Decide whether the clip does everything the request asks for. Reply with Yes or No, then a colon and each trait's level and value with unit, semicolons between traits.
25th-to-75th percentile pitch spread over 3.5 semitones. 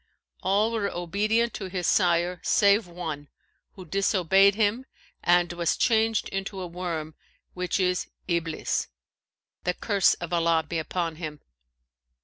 No: average, 2.9 semitones